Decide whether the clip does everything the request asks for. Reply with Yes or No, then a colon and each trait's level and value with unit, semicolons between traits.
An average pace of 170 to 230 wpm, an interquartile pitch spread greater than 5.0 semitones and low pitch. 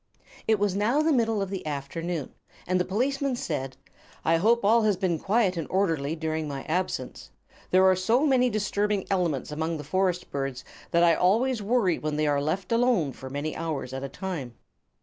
No: average, 190 wpm; wide, 5.5 semitones; medium, 180 Hz